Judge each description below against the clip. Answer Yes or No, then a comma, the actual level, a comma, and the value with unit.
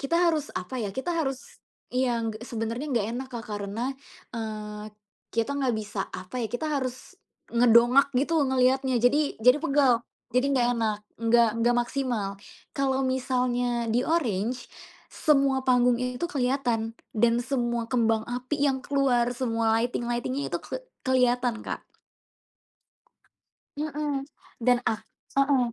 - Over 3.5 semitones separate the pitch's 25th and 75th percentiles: No, average, 2.7 semitones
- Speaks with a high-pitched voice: Yes, high, 245 Hz